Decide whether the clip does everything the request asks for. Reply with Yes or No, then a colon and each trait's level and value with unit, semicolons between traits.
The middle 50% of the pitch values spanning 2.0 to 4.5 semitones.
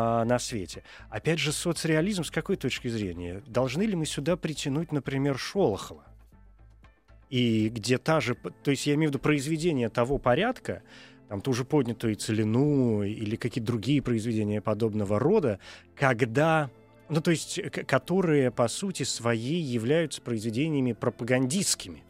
No: average, 5.2 semitones